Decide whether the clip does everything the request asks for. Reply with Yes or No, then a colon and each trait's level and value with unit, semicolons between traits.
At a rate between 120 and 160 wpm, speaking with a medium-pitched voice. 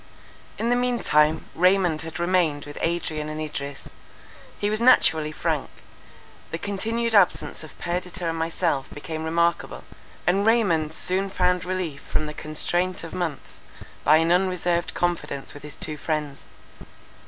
Yes: average, 145 wpm; medium, 170 Hz